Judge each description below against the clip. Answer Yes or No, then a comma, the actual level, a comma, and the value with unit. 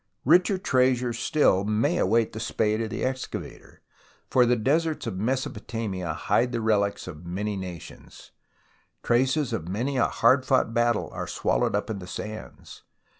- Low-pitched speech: Yes, low, 115 Hz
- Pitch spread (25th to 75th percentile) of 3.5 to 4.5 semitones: Yes, average, 4.1 semitones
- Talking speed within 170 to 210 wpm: No, average, 155 wpm